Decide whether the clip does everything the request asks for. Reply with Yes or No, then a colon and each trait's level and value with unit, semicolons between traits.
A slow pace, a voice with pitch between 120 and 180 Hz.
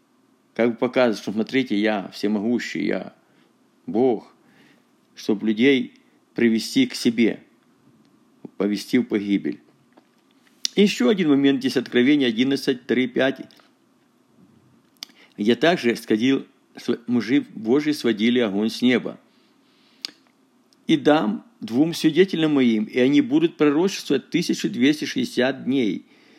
Yes: slow, 100 wpm; medium, 140 Hz